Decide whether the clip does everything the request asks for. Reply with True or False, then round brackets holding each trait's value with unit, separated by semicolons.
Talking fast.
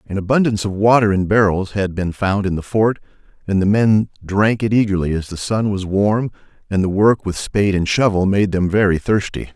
True (215 wpm)